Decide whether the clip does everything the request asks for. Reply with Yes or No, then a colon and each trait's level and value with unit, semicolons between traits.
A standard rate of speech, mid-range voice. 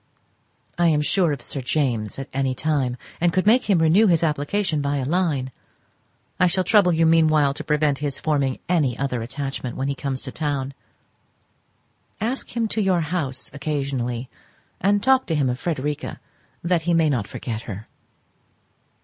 Yes: average, 170 wpm; medium, 150 Hz